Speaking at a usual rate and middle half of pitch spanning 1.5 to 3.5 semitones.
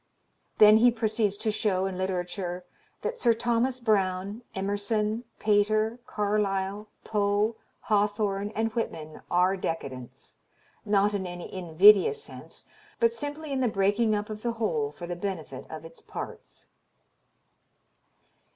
No: slow, 130 wpm; average, 2.9 semitones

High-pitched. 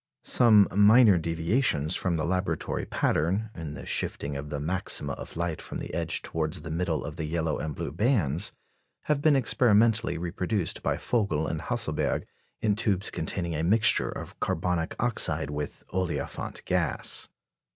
No: very low, 85 Hz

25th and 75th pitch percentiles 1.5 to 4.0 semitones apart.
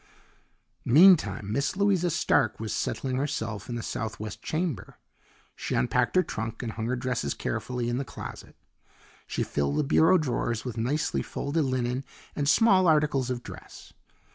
No: average, 5.2 semitones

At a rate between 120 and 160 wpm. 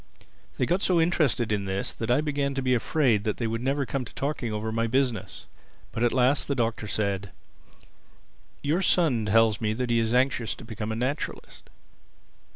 No: average, 190 wpm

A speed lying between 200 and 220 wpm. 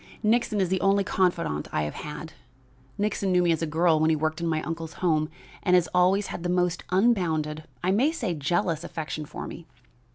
Yes: fast, 205 wpm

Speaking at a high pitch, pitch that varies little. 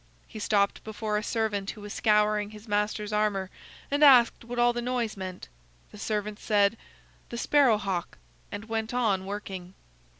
Yes: high, 210 Hz; narrow, 2.0 semitones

